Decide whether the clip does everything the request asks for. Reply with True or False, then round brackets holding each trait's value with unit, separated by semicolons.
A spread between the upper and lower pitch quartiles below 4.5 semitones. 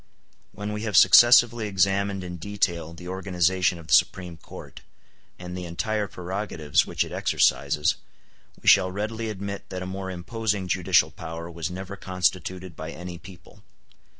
True (2.5 semitones)